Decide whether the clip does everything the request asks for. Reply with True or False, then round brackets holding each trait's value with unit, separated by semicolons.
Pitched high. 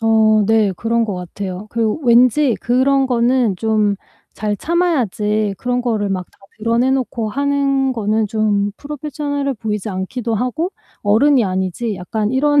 True (230 Hz)